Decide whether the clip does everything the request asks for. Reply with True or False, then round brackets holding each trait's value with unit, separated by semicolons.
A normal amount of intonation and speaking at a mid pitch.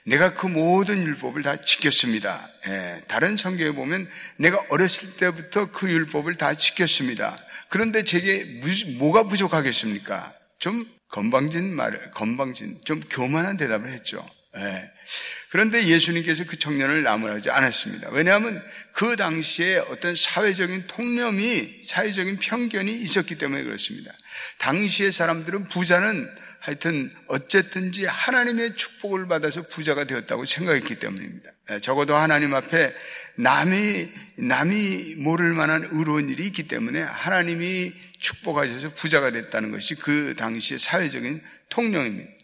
True (4.4 semitones; 175 Hz)